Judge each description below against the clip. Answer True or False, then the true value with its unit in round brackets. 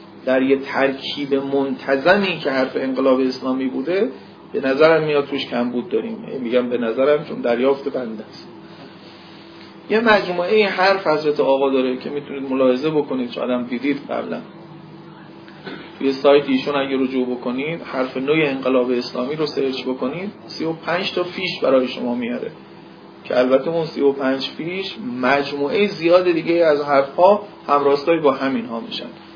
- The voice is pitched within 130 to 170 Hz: True (140 Hz)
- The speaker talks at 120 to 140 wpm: False (150 wpm)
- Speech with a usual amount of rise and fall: True (4.2 semitones)